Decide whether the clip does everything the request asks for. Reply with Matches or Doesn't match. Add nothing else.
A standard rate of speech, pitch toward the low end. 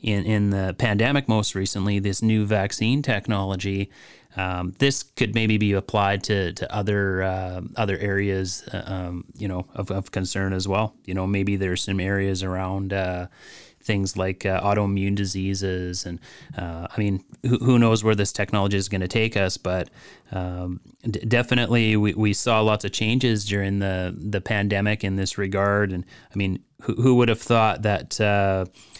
Matches